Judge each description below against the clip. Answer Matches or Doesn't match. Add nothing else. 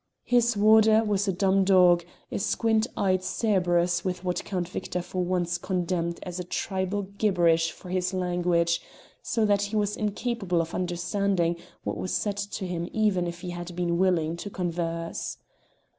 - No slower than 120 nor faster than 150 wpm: Doesn't match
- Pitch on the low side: Doesn't match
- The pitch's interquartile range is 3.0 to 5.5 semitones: Doesn't match